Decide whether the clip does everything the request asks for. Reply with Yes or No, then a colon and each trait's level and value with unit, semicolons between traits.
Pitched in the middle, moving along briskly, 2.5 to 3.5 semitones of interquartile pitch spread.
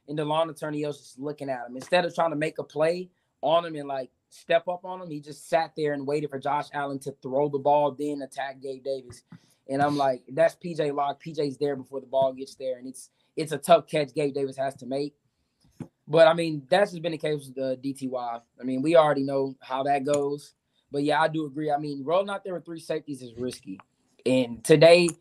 Yes: medium, 145 Hz; fast, 240 wpm; average, 2.9 semitones